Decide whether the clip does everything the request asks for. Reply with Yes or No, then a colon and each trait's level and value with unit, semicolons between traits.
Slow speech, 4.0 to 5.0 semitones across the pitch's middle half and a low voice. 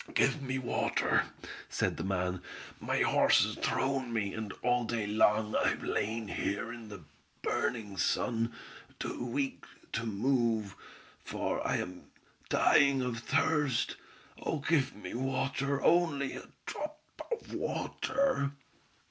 Yes: slow, 130 wpm; average, 4.3 semitones; low, 120 Hz